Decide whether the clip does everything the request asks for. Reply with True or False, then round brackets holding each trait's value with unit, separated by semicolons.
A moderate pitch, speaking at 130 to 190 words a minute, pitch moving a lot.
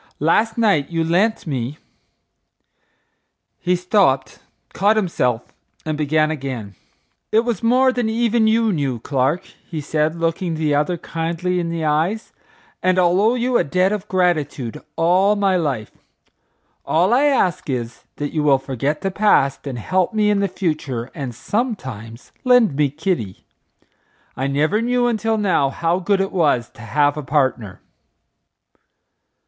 True (165 Hz; 150 wpm; 6.4 semitones)